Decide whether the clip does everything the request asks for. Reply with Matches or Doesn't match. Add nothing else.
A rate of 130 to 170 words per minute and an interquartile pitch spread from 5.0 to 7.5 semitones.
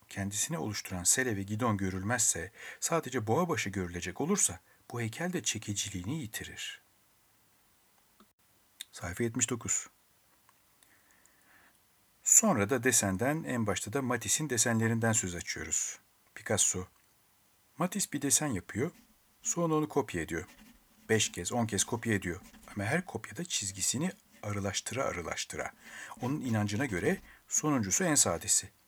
Doesn't match